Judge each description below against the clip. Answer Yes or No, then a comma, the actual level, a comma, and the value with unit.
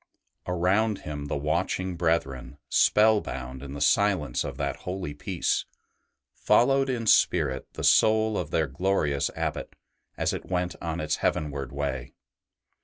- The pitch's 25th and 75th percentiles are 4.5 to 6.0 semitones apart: Yes, average, 5.3 semitones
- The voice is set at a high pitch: No, very low, 85 Hz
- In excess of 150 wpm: No, average, 140 wpm